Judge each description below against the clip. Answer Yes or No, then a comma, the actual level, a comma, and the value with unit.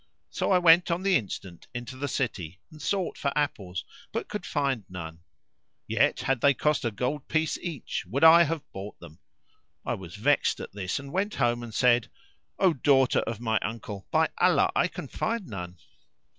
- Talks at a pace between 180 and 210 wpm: Yes, average, 185 wpm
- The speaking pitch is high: No, low, 130 Hz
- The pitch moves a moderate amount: No, wide, 7.2 semitones